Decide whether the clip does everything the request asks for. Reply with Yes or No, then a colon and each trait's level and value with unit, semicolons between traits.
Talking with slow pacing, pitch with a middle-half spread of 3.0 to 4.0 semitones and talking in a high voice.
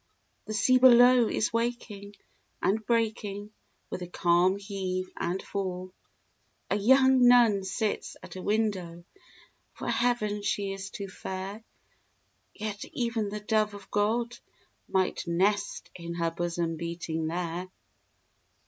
Yes: slow, 125 wpm; average, 3.3 semitones; high, 200 Hz